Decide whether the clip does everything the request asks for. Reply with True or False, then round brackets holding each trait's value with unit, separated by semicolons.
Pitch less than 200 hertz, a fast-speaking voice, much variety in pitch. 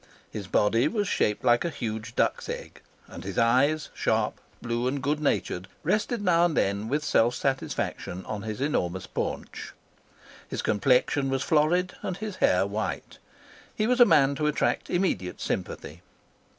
False (135 Hz; 160 wpm; 6.7 semitones)